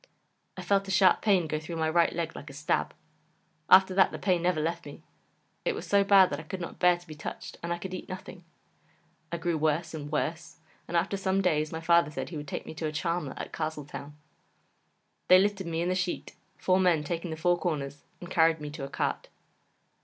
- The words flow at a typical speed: No, fast, 230 wpm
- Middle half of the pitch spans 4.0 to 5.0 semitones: No, average, 3.0 semitones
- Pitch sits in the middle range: Yes, medium, 170 Hz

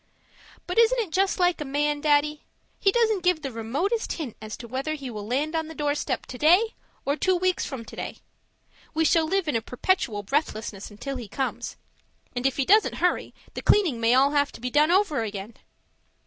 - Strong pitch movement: Yes, wide, 6.2 semitones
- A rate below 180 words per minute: No, average, 200 wpm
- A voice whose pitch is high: Yes, very high, 295 Hz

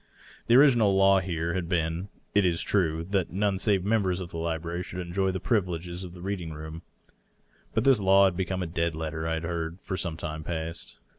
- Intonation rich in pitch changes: No, average, 2.8 semitones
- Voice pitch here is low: Yes, very low, 90 Hz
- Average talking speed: No, fast, 210 wpm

